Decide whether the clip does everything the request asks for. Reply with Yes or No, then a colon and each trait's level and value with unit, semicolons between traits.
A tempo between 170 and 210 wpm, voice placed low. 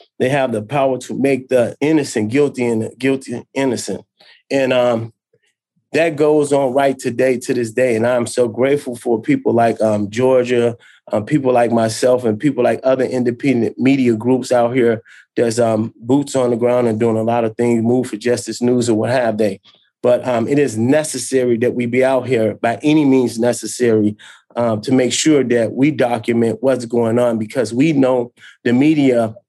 Yes: average, 190 wpm; low, 120 Hz